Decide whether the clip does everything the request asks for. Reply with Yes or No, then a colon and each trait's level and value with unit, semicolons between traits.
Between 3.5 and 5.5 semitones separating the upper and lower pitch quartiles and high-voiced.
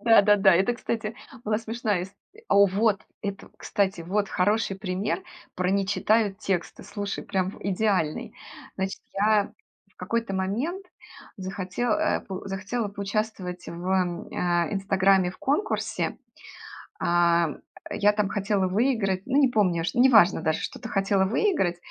No: narrow, 2.5 semitones; high, 195 Hz